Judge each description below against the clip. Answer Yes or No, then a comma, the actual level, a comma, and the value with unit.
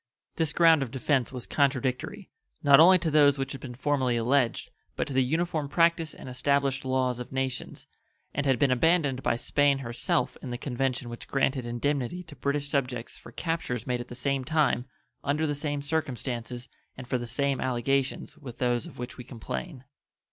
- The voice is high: No, low, 135 Hz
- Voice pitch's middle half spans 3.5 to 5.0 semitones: No, average, 2.8 semitones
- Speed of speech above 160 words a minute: Yes, average, 185 wpm